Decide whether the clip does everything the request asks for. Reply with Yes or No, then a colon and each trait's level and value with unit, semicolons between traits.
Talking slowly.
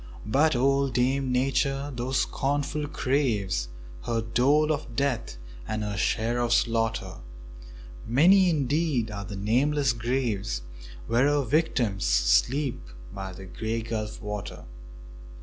Yes: slow, 120 wpm